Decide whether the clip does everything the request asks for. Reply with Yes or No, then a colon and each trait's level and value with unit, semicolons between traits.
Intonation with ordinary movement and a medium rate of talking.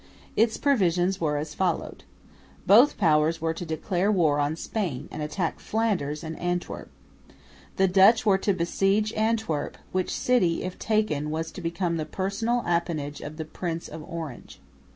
Yes: average, 4.1 semitones; average, 155 wpm